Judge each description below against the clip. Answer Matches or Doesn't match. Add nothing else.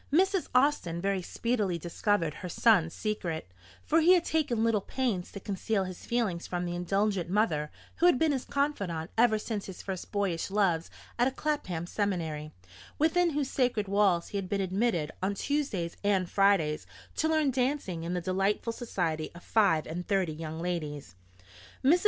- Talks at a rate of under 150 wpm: Doesn't match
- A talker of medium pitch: Doesn't match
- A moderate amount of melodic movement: Doesn't match